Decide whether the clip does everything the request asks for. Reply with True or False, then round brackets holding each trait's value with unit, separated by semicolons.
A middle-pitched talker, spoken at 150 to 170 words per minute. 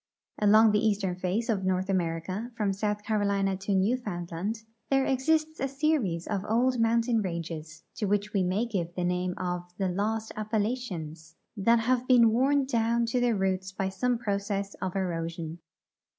False (205 Hz; 165 wpm)